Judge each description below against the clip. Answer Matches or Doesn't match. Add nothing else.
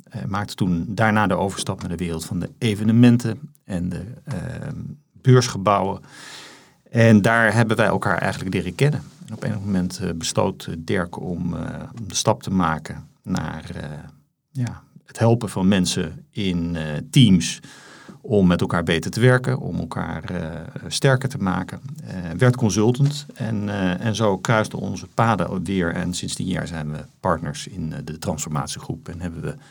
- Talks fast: Doesn't match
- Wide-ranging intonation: Matches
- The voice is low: Matches